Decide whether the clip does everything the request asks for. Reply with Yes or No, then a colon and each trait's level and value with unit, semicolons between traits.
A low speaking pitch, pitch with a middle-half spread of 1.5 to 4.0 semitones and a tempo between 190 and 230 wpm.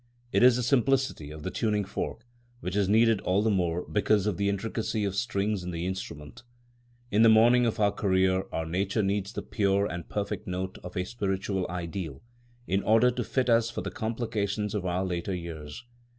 Yes: low, 100 Hz; average, 3.3 semitones; average, 200 wpm